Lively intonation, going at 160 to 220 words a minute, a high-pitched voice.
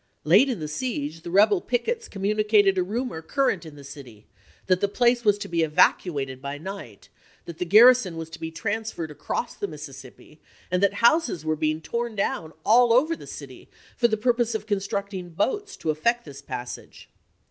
Yes: wide, 6.9 semitones; average, 190 wpm; high, 195 Hz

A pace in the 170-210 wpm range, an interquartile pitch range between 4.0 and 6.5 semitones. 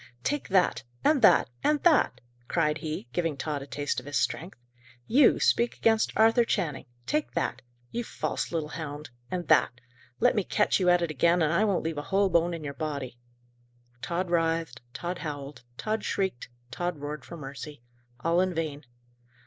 Yes: average, 180 wpm; average, 4.5 semitones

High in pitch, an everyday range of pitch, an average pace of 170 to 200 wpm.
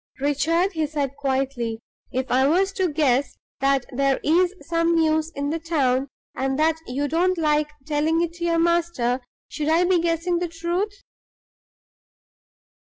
No: very high, 315 Hz; average, 3.6 semitones; average, 155 wpm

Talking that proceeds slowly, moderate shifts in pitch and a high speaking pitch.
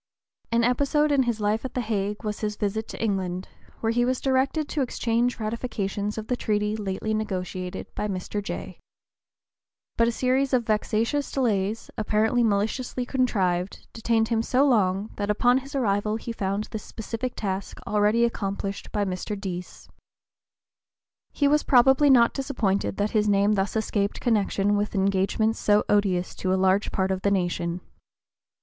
No: average, 160 wpm; average, 3.3 semitones; high, 215 Hz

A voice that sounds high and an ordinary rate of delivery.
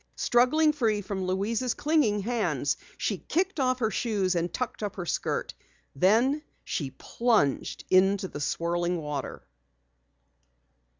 No: high, 210 Hz; slow, 125 wpm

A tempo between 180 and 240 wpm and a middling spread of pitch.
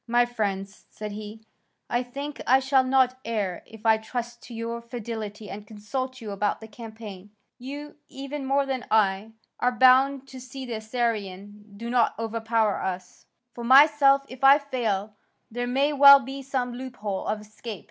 No: average, 170 wpm; average, 3.5 semitones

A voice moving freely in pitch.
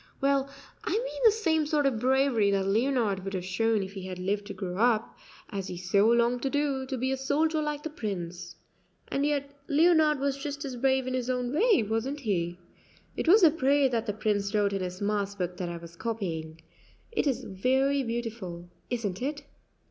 Yes: wide, 6.1 semitones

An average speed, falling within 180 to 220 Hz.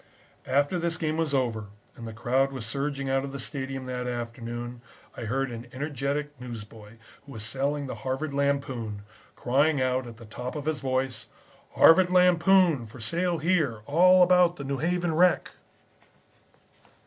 No: average, 160 wpm; low, 135 Hz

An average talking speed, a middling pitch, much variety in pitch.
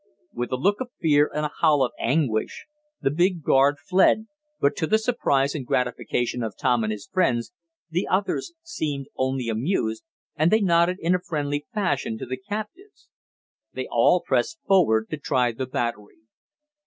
Yes: average, 170 wpm; medium, 145 Hz; wide, 6.8 semitones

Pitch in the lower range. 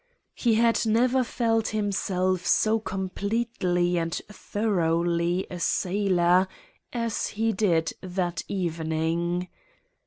No: medium, 185 Hz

